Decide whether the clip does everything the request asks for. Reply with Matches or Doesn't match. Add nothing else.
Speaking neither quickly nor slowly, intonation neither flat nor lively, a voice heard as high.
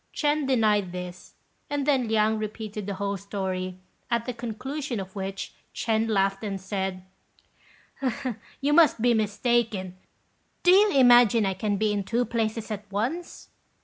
Matches